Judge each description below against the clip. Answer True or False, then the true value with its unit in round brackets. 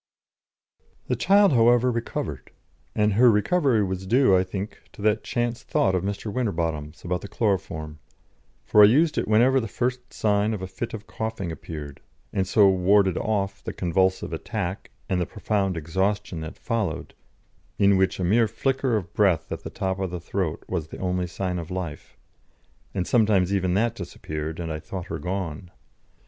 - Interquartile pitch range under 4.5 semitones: True (3.6 semitones)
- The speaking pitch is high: False (95 Hz)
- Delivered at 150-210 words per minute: True (180 wpm)